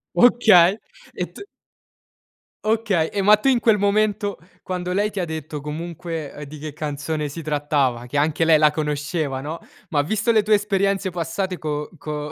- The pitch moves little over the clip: No, average, 5.2 semitones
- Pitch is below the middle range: No, medium, 165 Hz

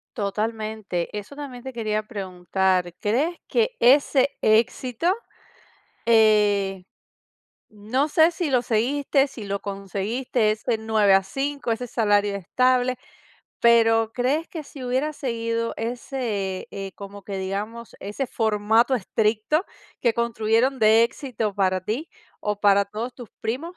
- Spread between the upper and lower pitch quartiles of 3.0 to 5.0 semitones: Yes, average, 3.7 semitones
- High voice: Yes, high, 225 Hz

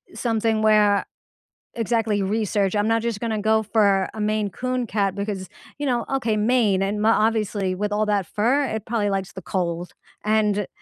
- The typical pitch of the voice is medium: No, high, 215 Hz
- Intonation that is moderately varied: No, narrow, 1.9 semitones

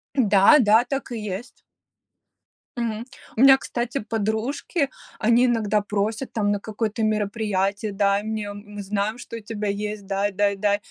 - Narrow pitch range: Yes, narrow, 2.2 semitones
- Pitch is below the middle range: No, high, 215 Hz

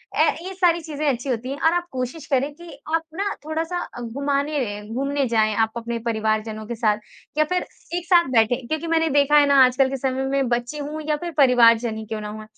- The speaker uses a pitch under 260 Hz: No, very high, 275 Hz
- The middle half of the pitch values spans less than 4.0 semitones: No, average, 5.0 semitones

